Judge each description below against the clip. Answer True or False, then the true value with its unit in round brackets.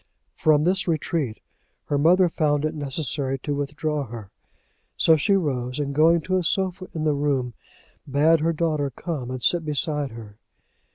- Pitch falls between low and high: True (150 Hz)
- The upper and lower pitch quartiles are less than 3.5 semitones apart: True (3.0 semitones)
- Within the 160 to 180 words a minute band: True (165 wpm)